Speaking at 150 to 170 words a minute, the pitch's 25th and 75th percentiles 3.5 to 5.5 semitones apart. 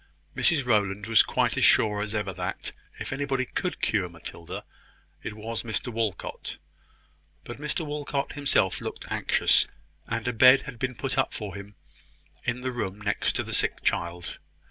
Yes: average, 165 wpm; average, 4.6 semitones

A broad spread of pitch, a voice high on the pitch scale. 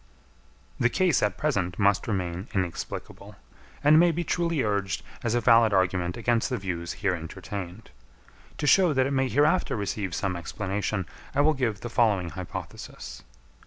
No: wide, 6.1 semitones; low, 105 Hz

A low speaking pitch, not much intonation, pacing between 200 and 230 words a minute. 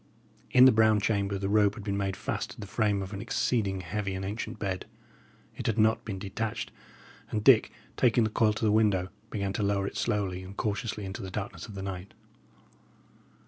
Yes: low, 100 Hz; narrow, 2.0 semitones; fast, 205 wpm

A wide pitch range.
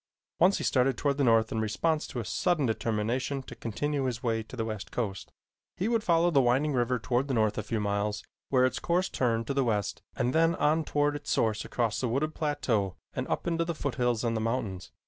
No: average, 4.7 semitones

